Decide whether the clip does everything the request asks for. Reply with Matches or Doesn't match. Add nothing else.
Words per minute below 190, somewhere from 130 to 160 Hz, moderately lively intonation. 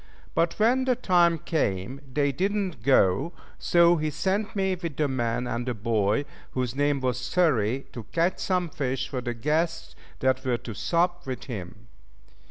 Doesn't match